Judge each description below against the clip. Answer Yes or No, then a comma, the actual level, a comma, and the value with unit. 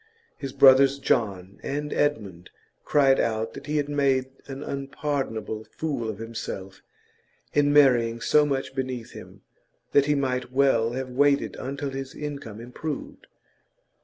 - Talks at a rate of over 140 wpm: No, slow, 135 wpm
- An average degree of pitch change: Yes, average, 3.6 semitones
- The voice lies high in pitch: No, low, 135 Hz